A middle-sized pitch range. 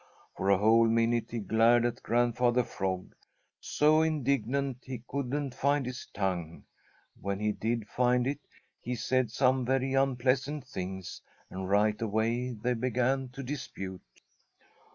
Yes: average, 3.5 semitones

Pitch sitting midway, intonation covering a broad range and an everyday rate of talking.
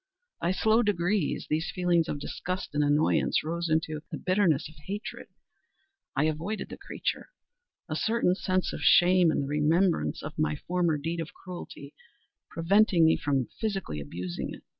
No: medium, 170 Hz; average, 3.4 semitones; average, 160 wpm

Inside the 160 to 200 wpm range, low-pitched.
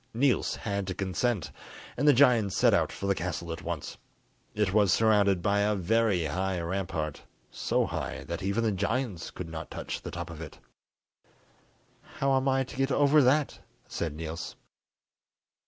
Yes: average, 170 wpm; low, 100 Hz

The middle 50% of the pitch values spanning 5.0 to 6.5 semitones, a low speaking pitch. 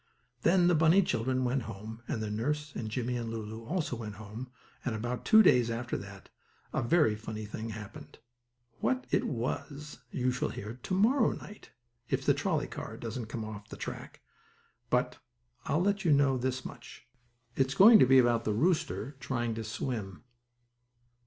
No: average, 4.5 semitones; low, 120 Hz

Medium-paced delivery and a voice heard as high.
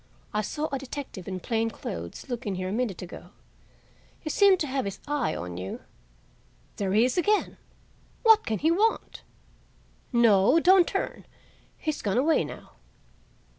Yes: average, 160 wpm; high, 240 Hz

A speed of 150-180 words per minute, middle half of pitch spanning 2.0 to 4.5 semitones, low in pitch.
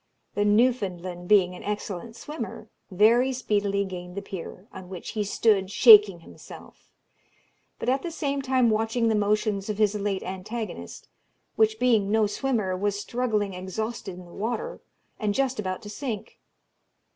No: average, 155 wpm; average, 3.2 semitones; high, 210 Hz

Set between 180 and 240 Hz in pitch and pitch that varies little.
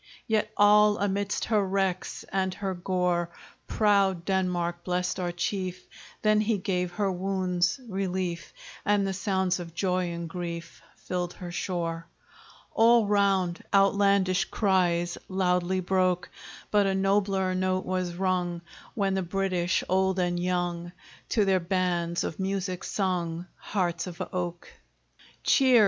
Yes: medium, 185 Hz; narrow, 1.9 semitones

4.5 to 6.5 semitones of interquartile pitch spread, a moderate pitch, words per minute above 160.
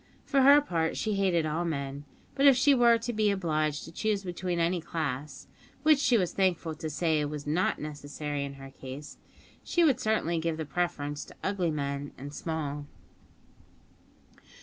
Yes: average, 5.3 semitones; medium, 165 Hz; average, 170 wpm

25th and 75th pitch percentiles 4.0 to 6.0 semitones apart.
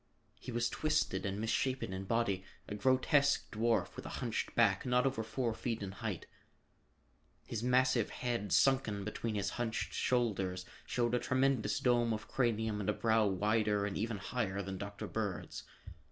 No: average, 3.4 semitones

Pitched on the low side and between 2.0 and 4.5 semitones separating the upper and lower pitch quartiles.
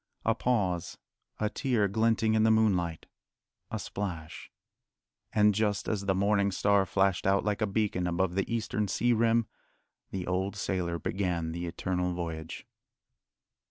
Yes: low, 100 Hz; average, 3.4 semitones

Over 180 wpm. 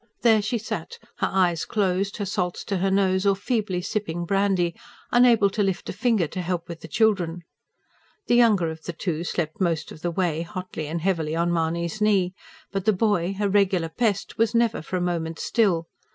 Yes: average, 195 wpm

